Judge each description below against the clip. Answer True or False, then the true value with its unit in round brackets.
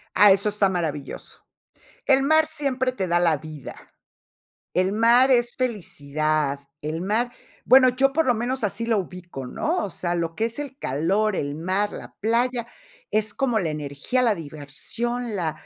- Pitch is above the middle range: True (210 Hz)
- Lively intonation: True (7.2 semitones)